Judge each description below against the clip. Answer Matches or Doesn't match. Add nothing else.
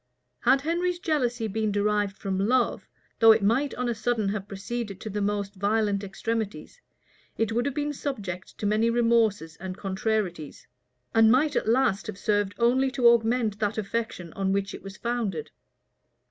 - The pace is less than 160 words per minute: Doesn't match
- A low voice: Doesn't match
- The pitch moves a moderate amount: Matches